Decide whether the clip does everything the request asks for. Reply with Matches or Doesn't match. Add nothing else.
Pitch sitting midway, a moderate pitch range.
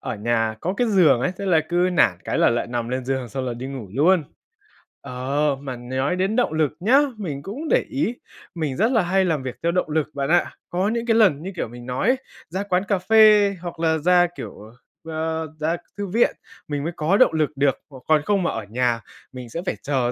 Doesn't match